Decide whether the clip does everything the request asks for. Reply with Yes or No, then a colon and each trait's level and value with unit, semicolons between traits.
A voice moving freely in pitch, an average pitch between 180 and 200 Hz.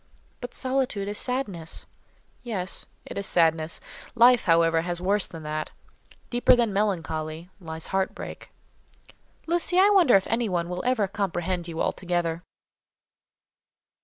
Yes: wide, 6.0 semitones; high, 190 Hz